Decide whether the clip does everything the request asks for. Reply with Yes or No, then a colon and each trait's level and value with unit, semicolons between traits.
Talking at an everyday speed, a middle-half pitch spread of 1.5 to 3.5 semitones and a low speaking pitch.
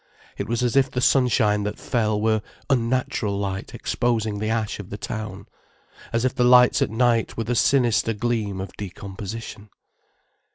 Yes: average, 165 wpm; average, 2.9 semitones; low, 110 Hz